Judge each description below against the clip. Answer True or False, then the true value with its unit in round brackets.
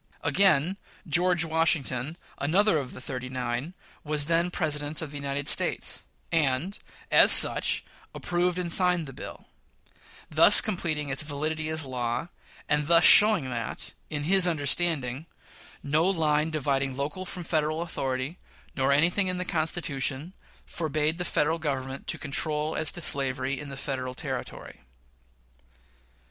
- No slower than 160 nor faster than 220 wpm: False (140 wpm)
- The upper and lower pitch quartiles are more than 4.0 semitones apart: False (3.6 semitones)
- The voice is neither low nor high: True (155 Hz)